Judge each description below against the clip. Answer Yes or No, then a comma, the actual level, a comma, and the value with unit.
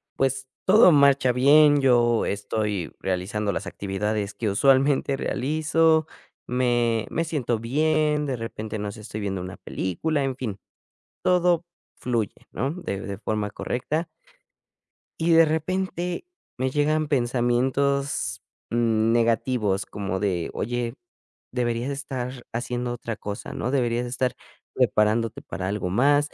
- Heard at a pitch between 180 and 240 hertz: No, low, 120 Hz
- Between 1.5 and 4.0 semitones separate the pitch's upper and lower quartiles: No, average, 4.9 semitones